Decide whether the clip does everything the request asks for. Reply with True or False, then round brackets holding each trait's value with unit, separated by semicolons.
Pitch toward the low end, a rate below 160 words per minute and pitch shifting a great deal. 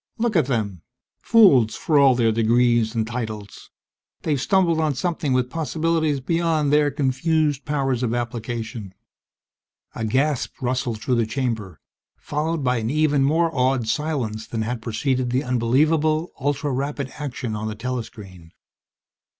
False (130 Hz; 140 wpm; 4.6 semitones)